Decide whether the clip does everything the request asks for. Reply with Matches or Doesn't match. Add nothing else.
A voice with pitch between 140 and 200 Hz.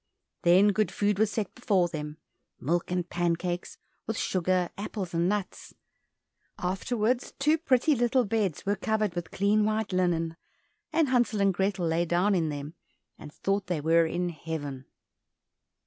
Matches